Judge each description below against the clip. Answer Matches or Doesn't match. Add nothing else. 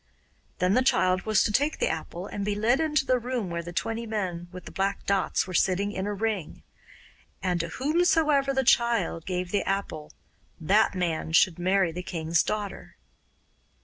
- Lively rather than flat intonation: Doesn't match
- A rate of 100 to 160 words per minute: Doesn't match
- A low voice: Doesn't match